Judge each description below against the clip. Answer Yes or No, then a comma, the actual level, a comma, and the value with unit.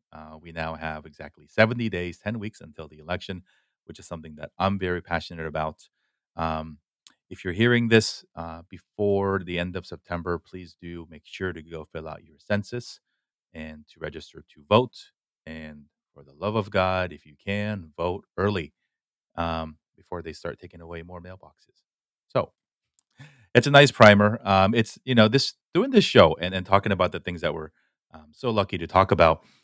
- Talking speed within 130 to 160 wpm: No, average, 185 wpm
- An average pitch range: Yes, average, 4.0 semitones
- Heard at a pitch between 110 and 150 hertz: No, very low, 90 Hz